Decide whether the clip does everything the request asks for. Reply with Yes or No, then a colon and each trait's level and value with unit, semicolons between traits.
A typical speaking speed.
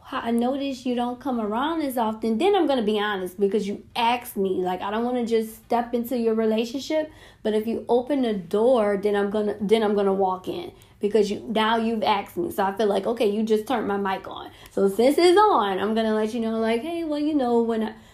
No: fast, 240 wpm